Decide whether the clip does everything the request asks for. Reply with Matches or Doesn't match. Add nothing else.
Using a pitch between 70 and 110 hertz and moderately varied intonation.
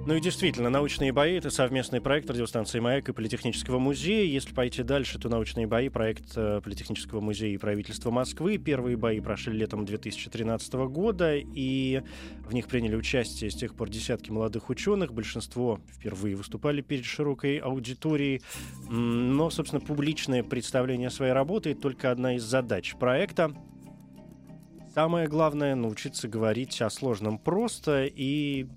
Doesn't match